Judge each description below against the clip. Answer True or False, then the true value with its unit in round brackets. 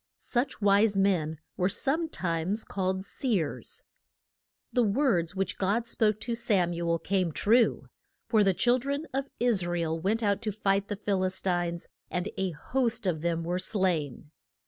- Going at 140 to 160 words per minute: False (170 wpm)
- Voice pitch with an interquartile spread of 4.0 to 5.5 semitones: True (4.5 semitones)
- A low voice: False (195 Hz)